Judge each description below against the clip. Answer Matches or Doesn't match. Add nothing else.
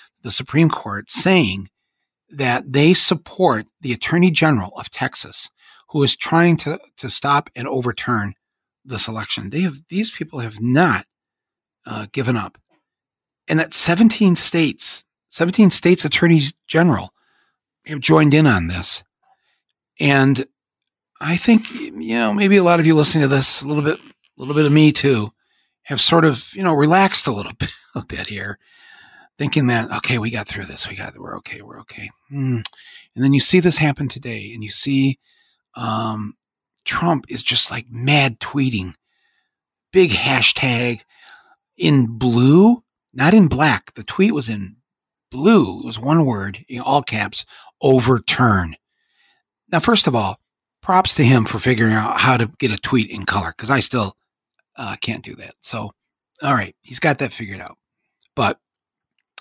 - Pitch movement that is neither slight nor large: Doesn't match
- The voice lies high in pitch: Doesn't match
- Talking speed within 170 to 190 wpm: Doesn't match